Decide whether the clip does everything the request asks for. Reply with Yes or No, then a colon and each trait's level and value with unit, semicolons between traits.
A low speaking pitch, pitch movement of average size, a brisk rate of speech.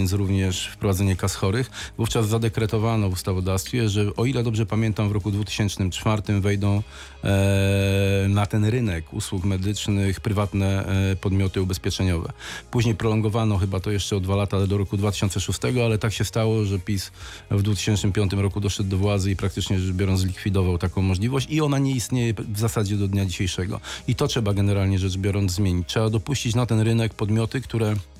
No: low, 100 Hz; narrow, 2.3 semitones; fast, 170 wpm